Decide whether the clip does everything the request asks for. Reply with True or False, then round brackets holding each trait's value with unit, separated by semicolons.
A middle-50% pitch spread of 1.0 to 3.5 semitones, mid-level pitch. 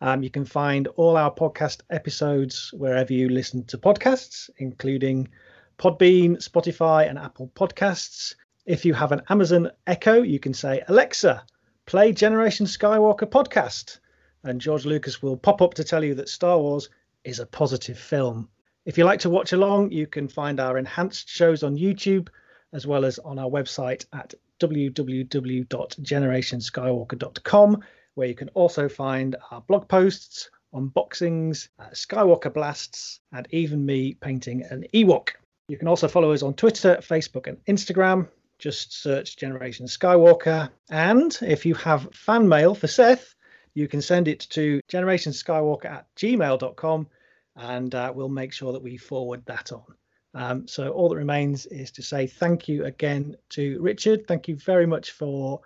False (4.9 semitones; 150 Hz)